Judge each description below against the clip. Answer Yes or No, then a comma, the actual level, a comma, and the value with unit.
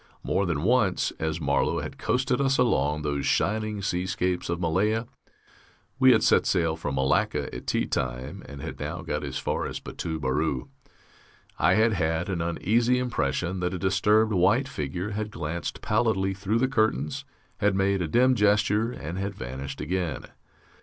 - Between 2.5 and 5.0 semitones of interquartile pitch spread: No, wide, 5.5 semitones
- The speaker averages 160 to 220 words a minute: Yes, average, 165 wpm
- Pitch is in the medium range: No, very low, 90 Hz